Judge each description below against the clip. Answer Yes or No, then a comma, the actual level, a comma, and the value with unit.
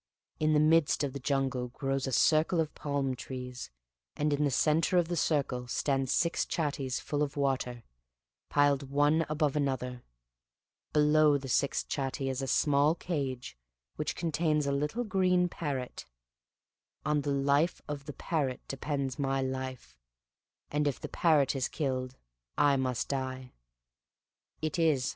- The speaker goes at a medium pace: Yes, average, 150 wpm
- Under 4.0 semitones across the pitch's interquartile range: Yes, narrow, 2.4 semitones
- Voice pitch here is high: No, medium, 140 Hz